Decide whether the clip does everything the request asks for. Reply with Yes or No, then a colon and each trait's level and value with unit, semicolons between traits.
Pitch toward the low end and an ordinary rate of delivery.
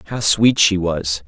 Yes: very low, 95 Hz; average, 190 wpm